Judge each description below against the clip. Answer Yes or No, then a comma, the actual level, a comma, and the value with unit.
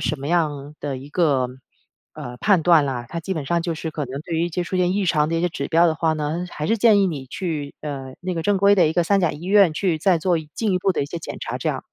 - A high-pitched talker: No, medium, 165 Hz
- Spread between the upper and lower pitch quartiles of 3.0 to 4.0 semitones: Yes, average, 3.5 semitones